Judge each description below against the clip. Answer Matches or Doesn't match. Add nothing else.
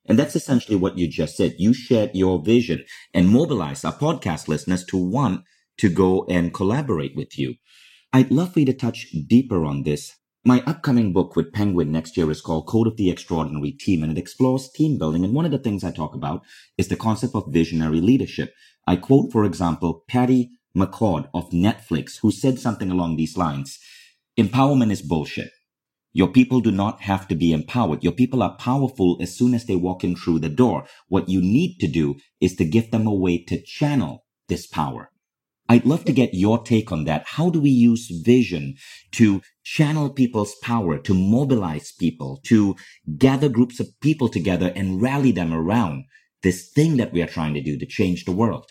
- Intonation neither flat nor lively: Doesn't match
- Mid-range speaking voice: Doesn't match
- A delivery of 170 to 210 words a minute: Matches